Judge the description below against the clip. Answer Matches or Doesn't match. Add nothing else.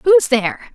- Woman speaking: Matches